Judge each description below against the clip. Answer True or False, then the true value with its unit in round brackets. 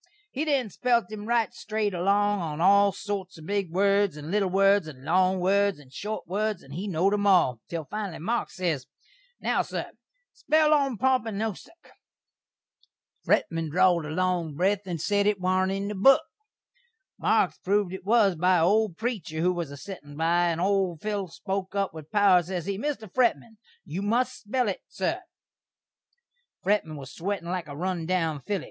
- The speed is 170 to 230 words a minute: True (180 wpm)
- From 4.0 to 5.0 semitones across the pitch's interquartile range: False (3.3 semitones)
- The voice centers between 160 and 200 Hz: True (190 Hz)